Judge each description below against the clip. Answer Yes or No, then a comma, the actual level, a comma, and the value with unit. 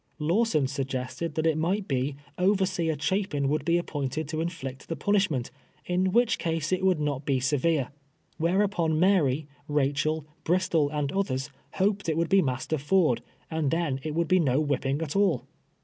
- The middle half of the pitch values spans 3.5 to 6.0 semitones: Yes, average, 4.2 semitones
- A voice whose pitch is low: No, medium, 155 Hz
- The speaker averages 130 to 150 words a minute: No, average, 170 wpm